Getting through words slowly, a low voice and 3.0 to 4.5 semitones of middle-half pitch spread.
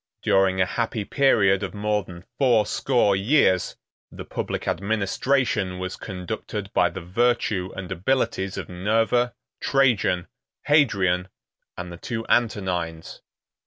Yes: slow, 120 wpm; low, 100 Hz; average, 4.2 semitones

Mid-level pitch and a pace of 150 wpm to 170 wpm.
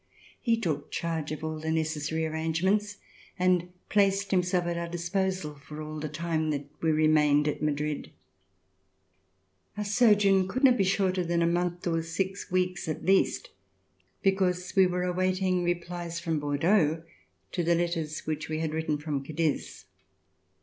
Yes: medium, 170 Hz; average, 155 wpm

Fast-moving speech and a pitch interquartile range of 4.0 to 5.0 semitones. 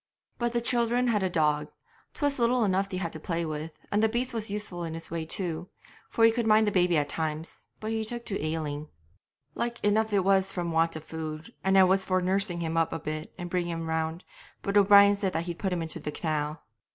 Yes: fast, 235 wpm; average, 4.5 semitones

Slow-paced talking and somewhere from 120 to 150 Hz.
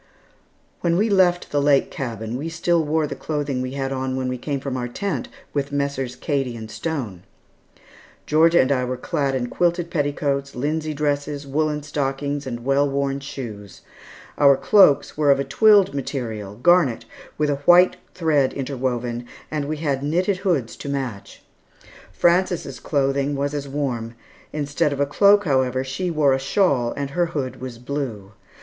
No: average, 165 wpm; medium, 140 Hz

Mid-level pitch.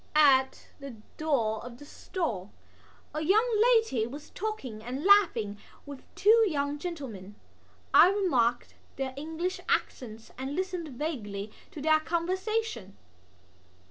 No: very high, 290 Hz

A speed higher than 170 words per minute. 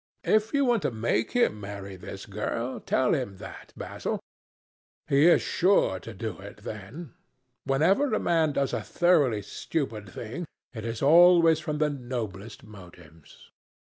No: average, 150 wpm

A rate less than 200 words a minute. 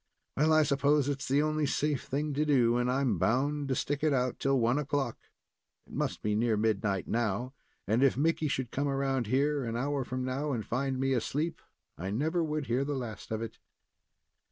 No: fast, 205 wpm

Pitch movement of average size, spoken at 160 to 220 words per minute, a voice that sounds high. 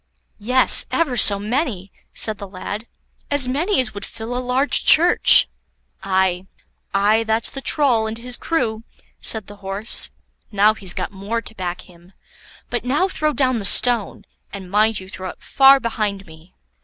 Yes: average, 4.2 semitones; average, 165 wpm; high, 220 Hz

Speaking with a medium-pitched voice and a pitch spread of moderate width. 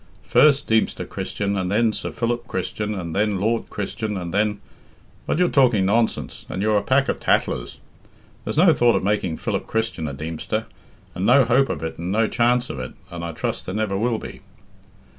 No: low, 105 Hz; average, 4.1 semitones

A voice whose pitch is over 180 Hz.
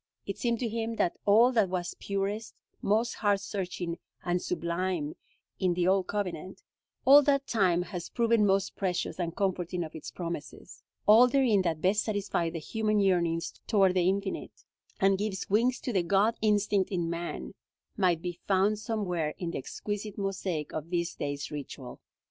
Yes: high, 190 Hz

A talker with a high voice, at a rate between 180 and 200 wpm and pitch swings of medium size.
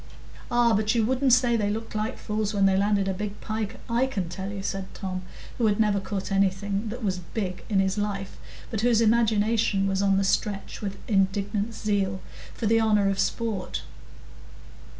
No: high, 205 Hz; average, 190 wpm; narrow, 2.2 semitones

